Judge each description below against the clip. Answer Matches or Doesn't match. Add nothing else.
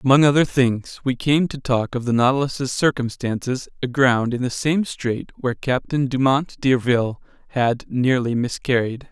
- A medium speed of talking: Matches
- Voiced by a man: Matches